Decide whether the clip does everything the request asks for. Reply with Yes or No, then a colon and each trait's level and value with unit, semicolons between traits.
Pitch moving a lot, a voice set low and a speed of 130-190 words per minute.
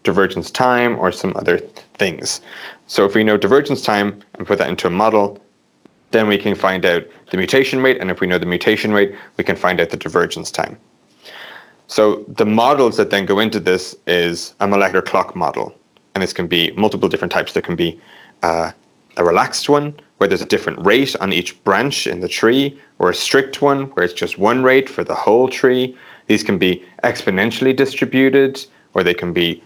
No: wide, 6.2 semitones; low, 105 Hz; average, 200 wpm